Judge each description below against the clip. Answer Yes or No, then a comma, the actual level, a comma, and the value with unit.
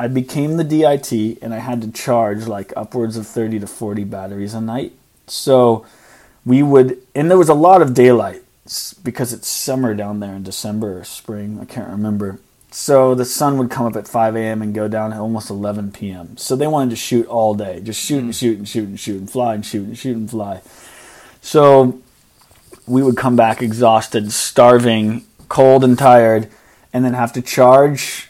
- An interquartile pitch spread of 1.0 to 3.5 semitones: Yes, average, 3.0 semitones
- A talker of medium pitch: No, low, 115 Hz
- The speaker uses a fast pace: No, average, 195 wpm